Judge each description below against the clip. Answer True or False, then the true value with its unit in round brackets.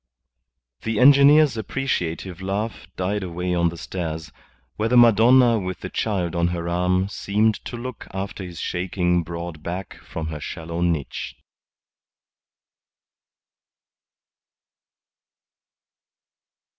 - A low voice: True (90 Hz)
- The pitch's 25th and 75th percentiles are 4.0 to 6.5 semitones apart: True (4.4 semitones)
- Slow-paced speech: True (105 wpm)